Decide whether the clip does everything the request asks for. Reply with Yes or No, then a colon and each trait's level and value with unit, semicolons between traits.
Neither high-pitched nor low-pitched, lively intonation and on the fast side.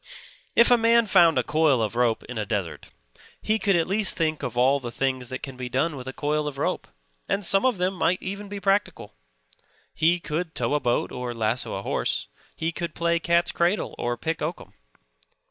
Yes: medium, 160 Hz; wide, 6.4 semitones; fast, 210 wpm